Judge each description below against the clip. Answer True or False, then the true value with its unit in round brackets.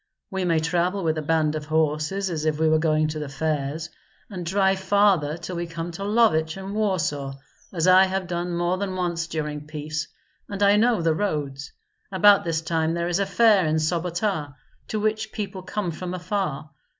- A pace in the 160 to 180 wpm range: False (195 wpm)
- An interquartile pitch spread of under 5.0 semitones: True (3.5 semitones)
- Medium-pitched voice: True (170 Hz)